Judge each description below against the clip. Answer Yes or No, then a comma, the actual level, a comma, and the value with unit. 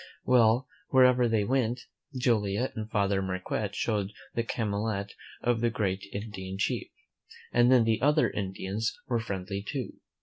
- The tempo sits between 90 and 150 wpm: Yes, average, 140 wpm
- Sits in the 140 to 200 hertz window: No, low, 110 Hz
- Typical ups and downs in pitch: Yes, average, 3.3 semitones